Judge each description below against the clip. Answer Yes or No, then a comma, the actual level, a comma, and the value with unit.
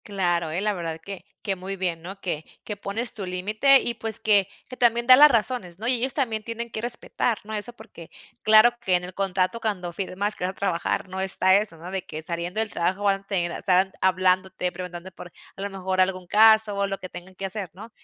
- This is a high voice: Yes, high, 195 Hz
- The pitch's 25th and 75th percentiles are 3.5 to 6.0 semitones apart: No, average, 3.1 semitones